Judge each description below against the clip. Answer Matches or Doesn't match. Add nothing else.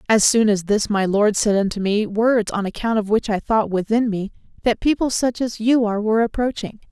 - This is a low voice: Doesn't match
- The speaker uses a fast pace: Matches